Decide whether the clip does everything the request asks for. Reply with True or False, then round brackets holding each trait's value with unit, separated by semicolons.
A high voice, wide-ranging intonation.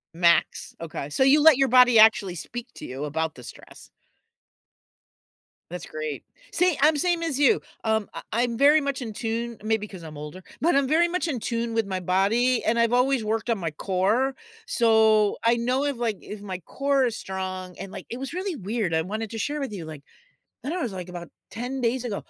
True (225 Hz; 5.9 semitones)